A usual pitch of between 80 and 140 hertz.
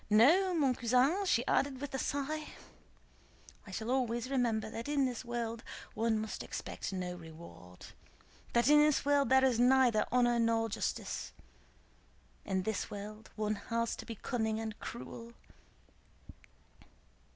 No: high, 235 Hz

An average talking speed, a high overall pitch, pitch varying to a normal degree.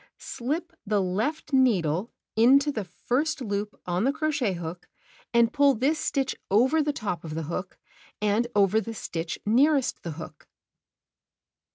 No: average, 150 wpm; high, 225 Hz; wide, 6.9 semitones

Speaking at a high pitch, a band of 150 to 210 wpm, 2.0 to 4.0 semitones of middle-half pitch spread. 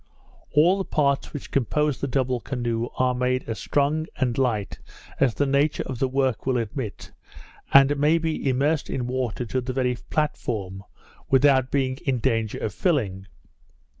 No: low, 130 Hz; average, 165 wpm; average, 2.7 semitones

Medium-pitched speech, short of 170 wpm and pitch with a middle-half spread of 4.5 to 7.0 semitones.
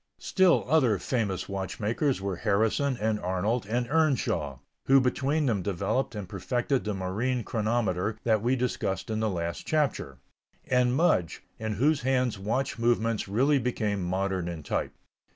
No: low, 110 Hz; average, 150 wpm; average, 4.8 semitones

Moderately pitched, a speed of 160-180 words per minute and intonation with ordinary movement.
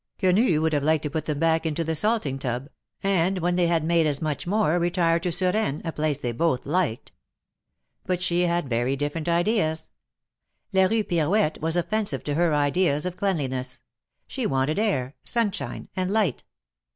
Yes: medium, 165 Hz; average, 175 wpm; average, 3.8 semitones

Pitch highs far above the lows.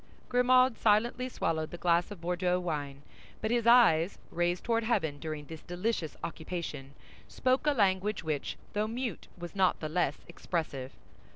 Yes: wide, 6.1 semitones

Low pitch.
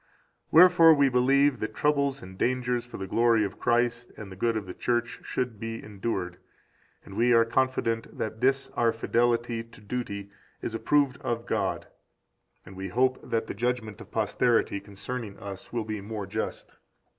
Yes: low, 115 Hz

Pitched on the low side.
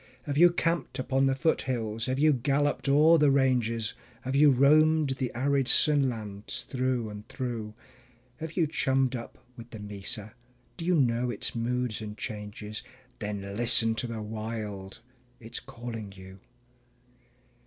Yes: low, 120 Hz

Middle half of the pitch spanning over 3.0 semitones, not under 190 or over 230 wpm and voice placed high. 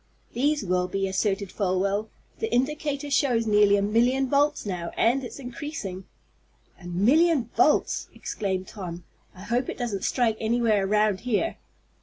No: average, 5.1 semitones; average, 145 wpm; high, 220 Hz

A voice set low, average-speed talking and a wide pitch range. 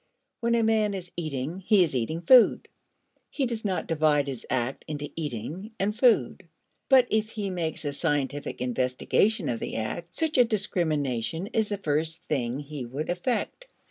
No: medium, 165 Hz; average, 170 wpm; wide, 6.9 semitones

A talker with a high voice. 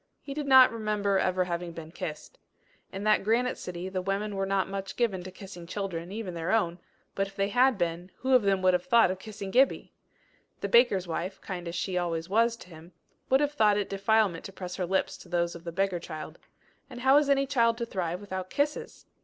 Yes: high, 195 Hz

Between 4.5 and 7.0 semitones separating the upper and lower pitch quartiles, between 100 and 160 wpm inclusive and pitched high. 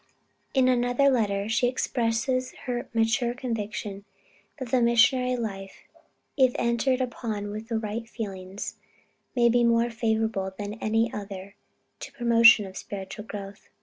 No: average, 2.9 semitones; slow, 135 wpm; high, 230 Hz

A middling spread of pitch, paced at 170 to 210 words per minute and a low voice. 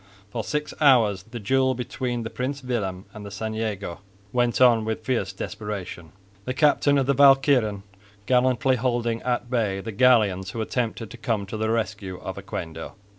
Yes: average, 3.6 semitones; average, 175 wpm; low, 115 Hz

